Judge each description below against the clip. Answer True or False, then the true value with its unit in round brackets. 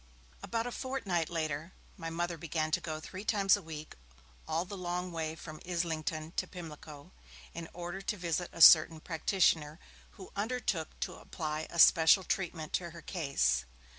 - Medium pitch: True (170 Hz)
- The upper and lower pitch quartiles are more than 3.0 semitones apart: False (2.7 semitones)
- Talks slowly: False (165 wpm)